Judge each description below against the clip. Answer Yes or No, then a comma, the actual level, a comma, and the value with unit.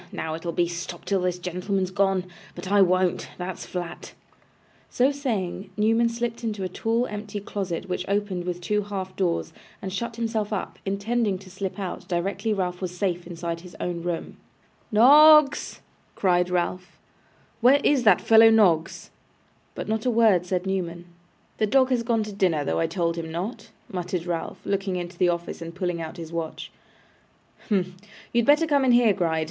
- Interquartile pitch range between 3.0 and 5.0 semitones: Yes, average, 3.8 semitones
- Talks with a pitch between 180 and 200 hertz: Yes, high, 190 Hz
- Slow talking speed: No, average, 180 wpm